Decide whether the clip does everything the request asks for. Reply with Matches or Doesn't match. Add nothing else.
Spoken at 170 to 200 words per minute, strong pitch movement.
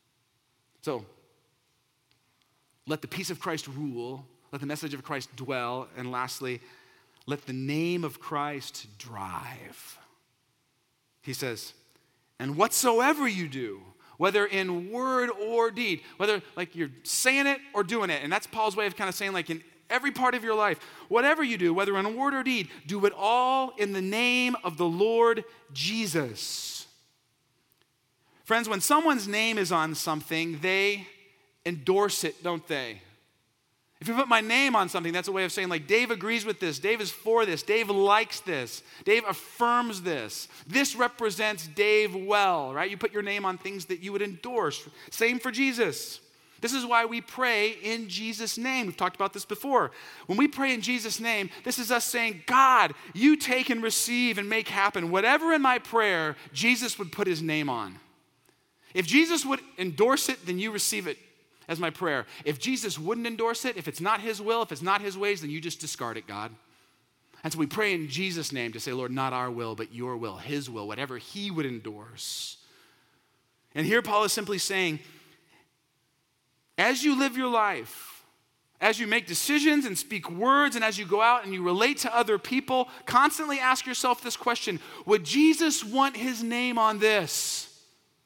Matches